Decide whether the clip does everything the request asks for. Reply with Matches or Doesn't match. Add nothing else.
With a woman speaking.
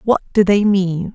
Matches